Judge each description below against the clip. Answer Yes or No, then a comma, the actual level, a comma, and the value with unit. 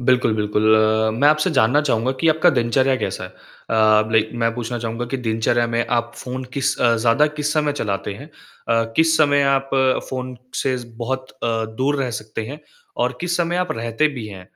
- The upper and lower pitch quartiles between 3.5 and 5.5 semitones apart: Yes, average, 4.0 semitones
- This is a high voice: No, low, 125 Hz